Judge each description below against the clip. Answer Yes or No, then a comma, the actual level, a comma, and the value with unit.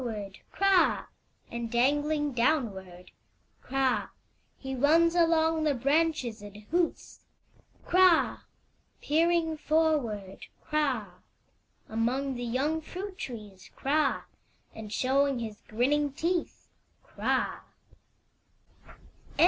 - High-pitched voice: Yes, very high, 275 Hz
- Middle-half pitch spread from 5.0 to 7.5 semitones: Yes, wide, 5.5 semitones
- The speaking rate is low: Yes, slow, 90 wpm